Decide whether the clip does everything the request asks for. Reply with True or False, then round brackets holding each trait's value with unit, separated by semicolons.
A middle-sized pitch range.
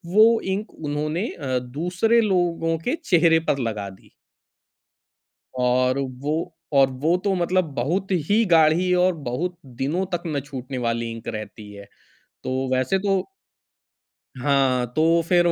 False (5.7 semitones)